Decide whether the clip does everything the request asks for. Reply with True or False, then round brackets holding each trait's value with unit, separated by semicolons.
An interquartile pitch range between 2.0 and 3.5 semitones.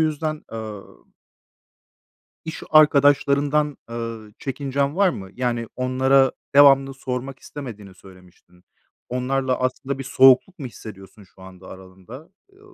False (4.6 semitones)